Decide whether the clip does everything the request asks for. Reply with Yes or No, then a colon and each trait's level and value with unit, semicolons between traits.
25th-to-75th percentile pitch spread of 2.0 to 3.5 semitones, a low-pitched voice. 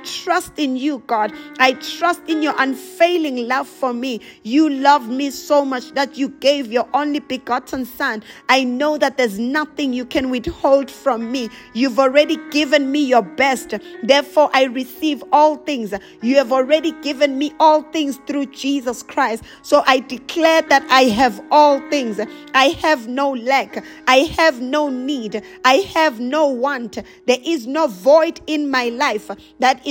No: average, 2.8 semitones; very high, 275 Hz